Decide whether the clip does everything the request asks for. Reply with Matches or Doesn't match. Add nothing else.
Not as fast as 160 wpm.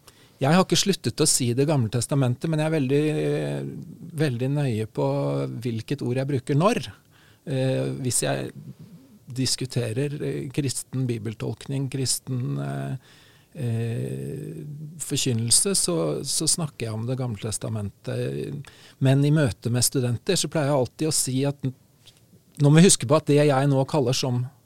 Matches